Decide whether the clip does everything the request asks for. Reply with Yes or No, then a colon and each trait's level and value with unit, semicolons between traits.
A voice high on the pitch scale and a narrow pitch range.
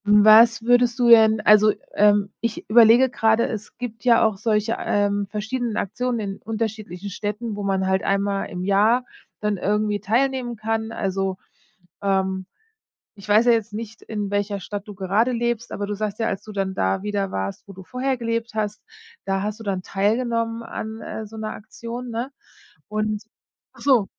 Yes: high, 215 Hz; narrow, 2.3 semitones